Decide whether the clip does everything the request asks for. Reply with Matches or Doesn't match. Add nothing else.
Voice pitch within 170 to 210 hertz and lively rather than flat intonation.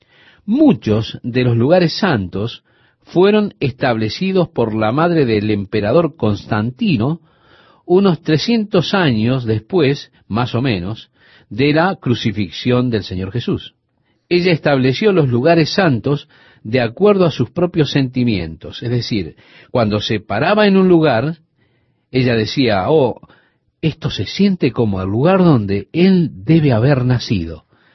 Doesn't match